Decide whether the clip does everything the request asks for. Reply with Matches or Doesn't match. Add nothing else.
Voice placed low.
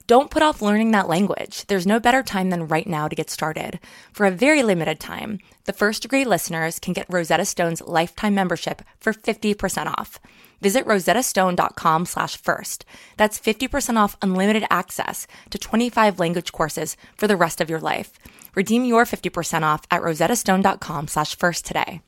Doesn't match